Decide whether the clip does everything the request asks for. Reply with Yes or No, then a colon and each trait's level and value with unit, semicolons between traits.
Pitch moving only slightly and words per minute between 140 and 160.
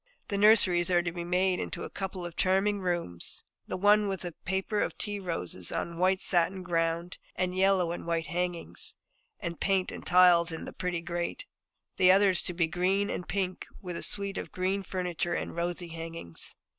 No: narrow, 2.0 semitones; average, 195 wpm